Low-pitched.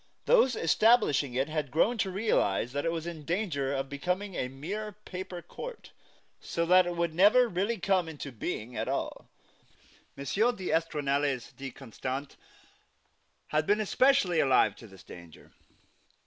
No: medium, 165 Hz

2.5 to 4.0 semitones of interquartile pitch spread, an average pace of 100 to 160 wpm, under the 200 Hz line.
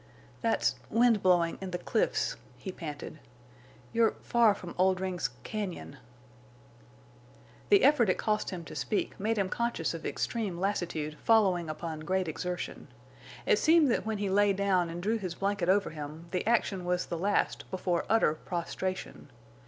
Yes: average, 3.5 semitones; average, 145 wpm; medium, 185 Hz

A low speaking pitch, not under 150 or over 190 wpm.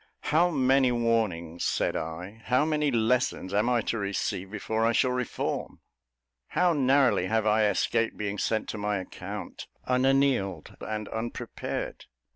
No: low, 115 Hz; average, 140 wpm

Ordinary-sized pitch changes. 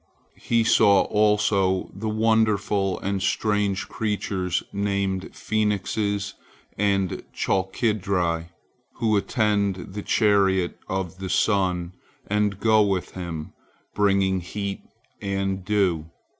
No: narrow, 1.7 semitones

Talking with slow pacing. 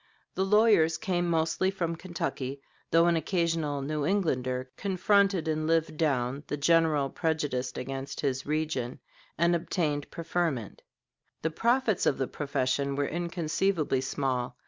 Yes: slow, 130 wpm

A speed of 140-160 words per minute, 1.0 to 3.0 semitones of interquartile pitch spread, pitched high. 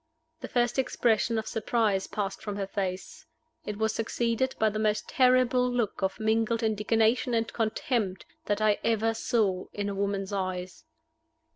Yes: average, 155 wpm; narrow, 2.5 semitones; high, 220 Hz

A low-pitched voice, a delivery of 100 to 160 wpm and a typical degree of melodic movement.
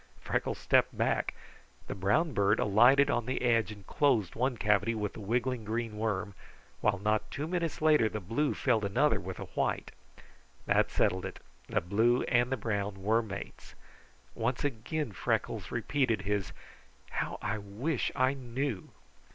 Yes: low, 115 Hz; average, 155 wpm; average, 4.1 semitones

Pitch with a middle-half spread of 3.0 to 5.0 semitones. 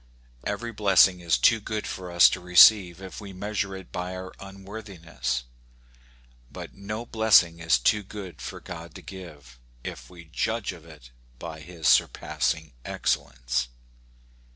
Yes: average, 3.6 semitones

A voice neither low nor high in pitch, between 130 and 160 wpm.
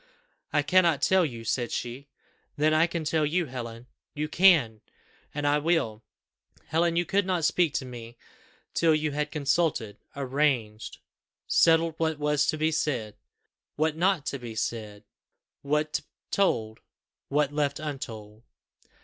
Yes: medium, 150 Hz; average, 140 wpm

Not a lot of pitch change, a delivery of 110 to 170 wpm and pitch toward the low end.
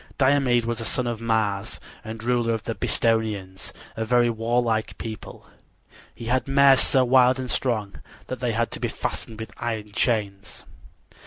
Yes: narrow, 2.0 semitones; average, 165 wpm; low, 115 Hz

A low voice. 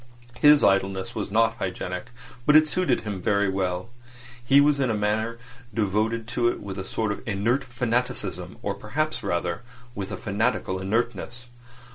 Yes: low, 110 Hz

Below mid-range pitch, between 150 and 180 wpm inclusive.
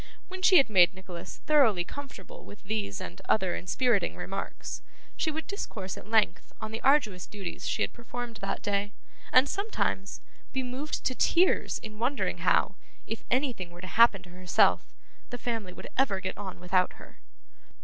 No: high, 215 Hz; average, 170 wpm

